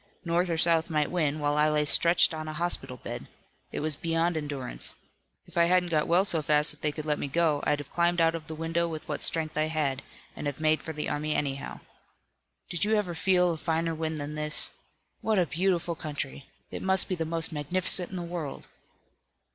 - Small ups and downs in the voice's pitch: Yes, narrow, 2.2 semitones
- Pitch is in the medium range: Yes, medium, 160 Hz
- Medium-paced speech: No, fast, 220 wpm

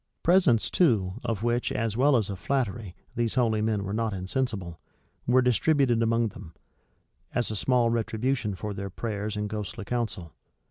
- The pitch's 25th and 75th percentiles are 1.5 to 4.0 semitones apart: Yes, average, 3.1 semitones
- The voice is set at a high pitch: No, low, 115 Hz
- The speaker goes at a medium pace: Yes, average, 160 wpm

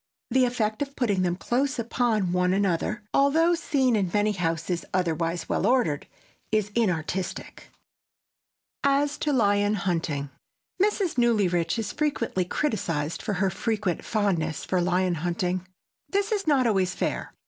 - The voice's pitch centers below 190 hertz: No, high, 205 Hz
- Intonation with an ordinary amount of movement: No, wide, 5.7 semitones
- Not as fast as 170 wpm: Yes, average, 140 wpm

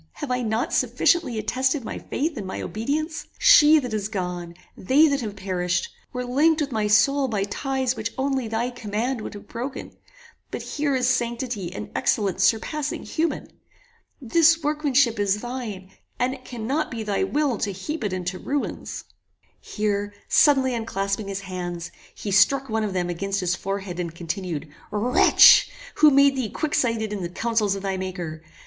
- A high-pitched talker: Yes, high, 225 Hz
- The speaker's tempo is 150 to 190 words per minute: Yes, average, 170 wpm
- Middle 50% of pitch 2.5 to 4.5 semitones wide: No, wide, 5.5 semitones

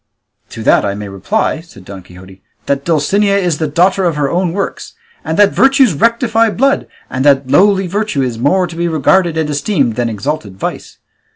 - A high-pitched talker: No, medium, 160 Hz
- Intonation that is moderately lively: No, wide, 7.1 semitones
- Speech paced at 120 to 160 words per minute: No, average, 190 wpm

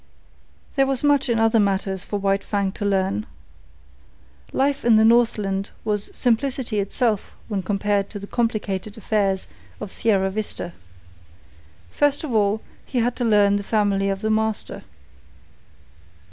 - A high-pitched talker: Yes, high, 210 Hz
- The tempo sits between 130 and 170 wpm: Yes, average, 145 wpm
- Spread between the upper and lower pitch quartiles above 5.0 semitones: No, average, 2.7 semitones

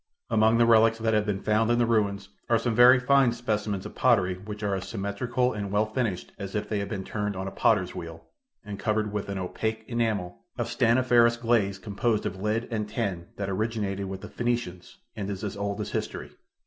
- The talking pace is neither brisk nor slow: No, fast, 210 wpm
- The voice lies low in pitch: Yes, low, 105 Hz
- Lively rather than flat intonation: No, narrow, 2.6 semitones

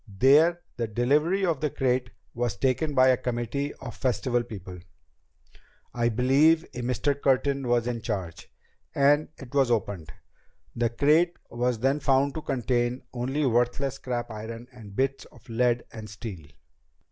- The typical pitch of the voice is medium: No, low, 125 Hz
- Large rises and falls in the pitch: No, average, 2.9 semitones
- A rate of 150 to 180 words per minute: Yes, average, 155 wpm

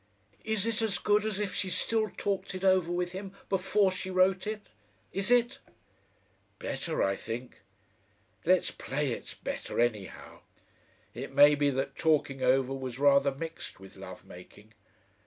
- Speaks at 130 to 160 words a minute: Yes, average, 155 wpm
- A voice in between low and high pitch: Yes, medium, 175 Hz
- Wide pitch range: Yes, wide, 6.7 semitones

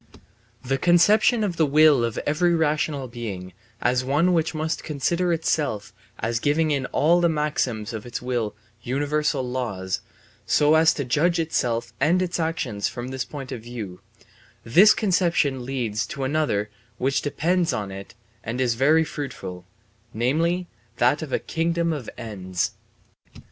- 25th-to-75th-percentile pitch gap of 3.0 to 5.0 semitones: No, wide, 5.4 semitones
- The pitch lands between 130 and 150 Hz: Yes, medium, 140 Hz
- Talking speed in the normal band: Yes, average, 150 wpm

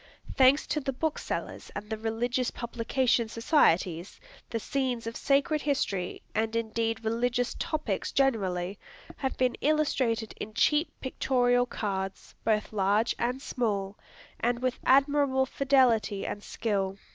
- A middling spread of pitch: Yes, average, 3.6 semitones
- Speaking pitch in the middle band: No, high, 235 Hz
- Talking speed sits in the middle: No, slow, 125 wpm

